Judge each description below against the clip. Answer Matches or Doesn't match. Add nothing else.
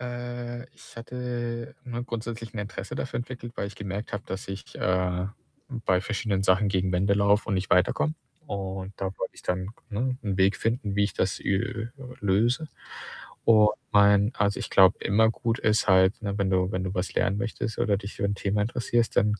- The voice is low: Matches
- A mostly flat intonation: Doesn't match